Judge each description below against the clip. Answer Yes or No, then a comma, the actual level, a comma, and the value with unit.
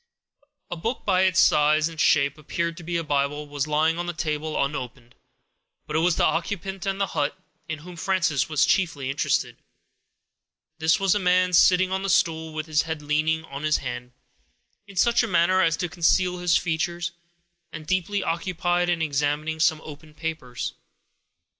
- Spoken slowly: No, average, 180 wpm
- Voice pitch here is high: No, medium, 160 Hz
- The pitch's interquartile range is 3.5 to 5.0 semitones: No, average, 2.9 semitones